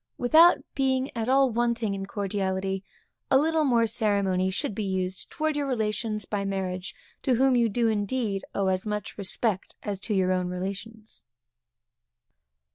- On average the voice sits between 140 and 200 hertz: No, high, 210 Hz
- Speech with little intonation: No, average, 4.0 semitones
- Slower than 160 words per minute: Yes, average, 150 wpm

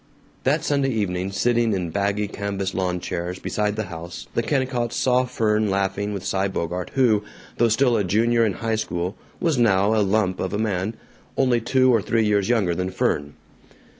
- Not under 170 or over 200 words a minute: Yes, average, 185 wpm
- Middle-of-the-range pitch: No, low, 105 Hz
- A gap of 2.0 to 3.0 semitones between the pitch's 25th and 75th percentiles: No, average, 3.7 semitones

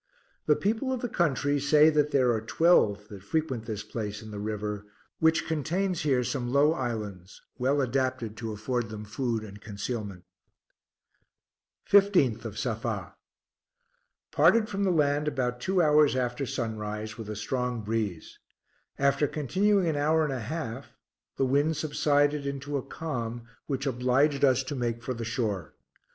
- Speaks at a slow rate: No, average, 155 wpm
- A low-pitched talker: Yes, low, 130 Hz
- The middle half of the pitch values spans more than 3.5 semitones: Yes, average, 5.2 semitones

